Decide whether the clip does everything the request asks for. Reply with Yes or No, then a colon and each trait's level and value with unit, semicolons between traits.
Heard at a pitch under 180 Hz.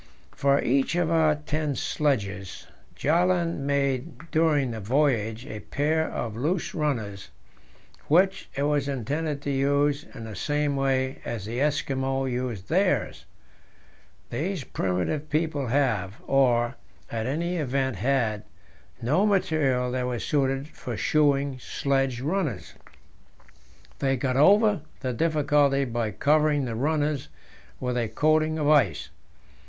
Yes: medium, 140 Hz